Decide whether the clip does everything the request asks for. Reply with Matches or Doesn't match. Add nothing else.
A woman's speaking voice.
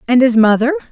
Matches